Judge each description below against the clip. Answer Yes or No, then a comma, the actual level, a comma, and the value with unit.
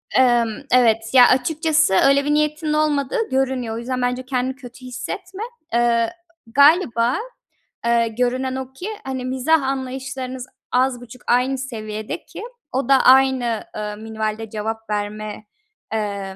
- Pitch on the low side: No, very high, 255 Hz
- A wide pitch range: No, average, 2.8 semitones